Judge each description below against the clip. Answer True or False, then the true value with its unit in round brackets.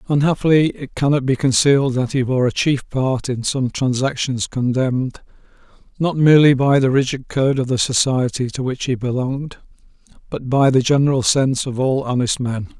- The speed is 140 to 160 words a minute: False (175 wpm)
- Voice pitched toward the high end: False (130 Hz)